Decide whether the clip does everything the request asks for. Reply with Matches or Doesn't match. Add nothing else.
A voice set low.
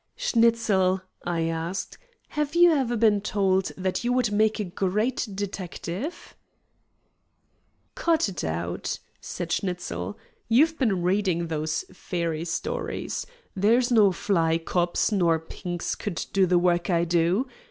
Doesn't match